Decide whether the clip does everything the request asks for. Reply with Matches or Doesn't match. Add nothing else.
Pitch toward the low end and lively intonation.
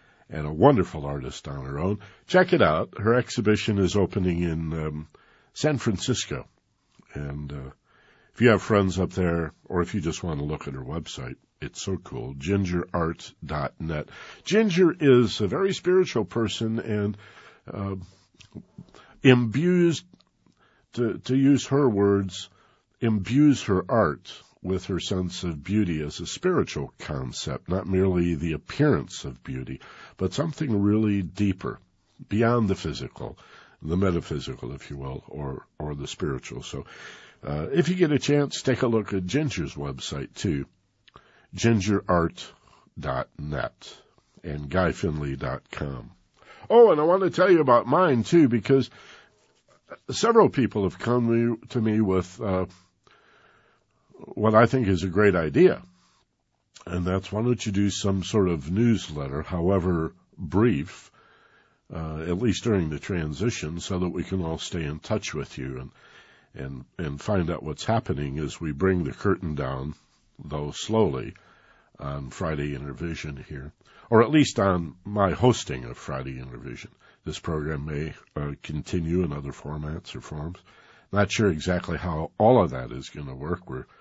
Matches